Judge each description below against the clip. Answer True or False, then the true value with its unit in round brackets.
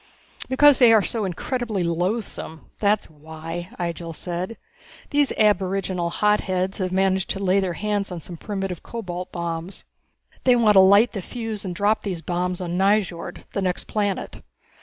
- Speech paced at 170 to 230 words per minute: False (160 wpm)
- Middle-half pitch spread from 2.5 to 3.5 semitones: True (3.1 semitones)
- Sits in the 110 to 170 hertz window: False (190 Hz)